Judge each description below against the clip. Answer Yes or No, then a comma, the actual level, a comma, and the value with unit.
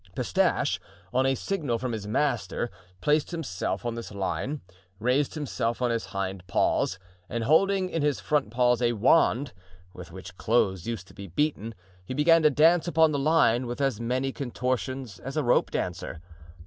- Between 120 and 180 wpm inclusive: Yes, average, 175 wpm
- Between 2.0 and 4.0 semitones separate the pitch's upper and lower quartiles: No, average, 5.2 semitones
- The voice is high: No, low, 125 Hz